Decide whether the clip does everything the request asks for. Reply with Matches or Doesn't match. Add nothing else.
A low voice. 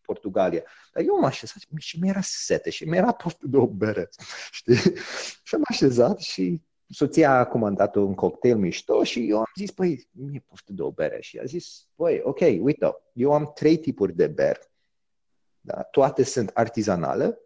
Doesn't match